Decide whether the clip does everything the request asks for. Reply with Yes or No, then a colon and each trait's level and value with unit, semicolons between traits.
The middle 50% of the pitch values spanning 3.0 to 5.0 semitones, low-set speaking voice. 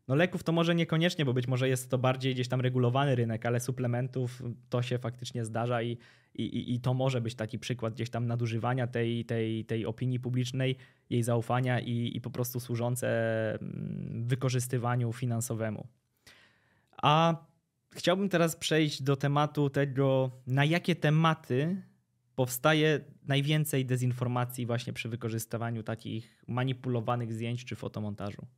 No: narrow, 2.6 semitones; low, 125 Hz